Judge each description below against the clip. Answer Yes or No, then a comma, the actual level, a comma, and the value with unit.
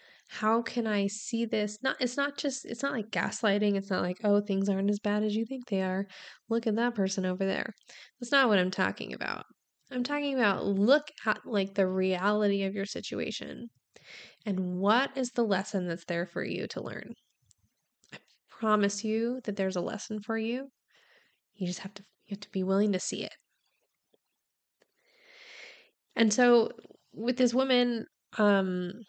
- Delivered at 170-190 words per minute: Yes, average, 180 wpm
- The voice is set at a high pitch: Yes, high, 215 Hz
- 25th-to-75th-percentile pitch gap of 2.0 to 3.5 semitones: No, average, 3.9 semitones